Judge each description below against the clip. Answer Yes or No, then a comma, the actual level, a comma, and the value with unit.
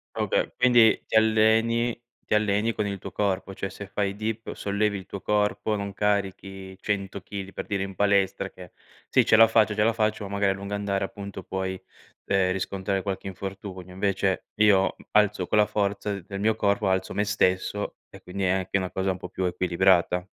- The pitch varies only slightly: Yes, narrow, 1.7 semitones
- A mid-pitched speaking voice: No, low, 100 Hz